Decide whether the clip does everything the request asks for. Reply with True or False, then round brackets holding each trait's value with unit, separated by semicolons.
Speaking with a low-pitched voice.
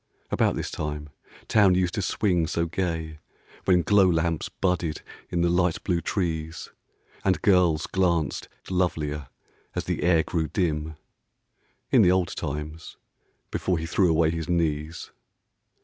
True (85 Hz)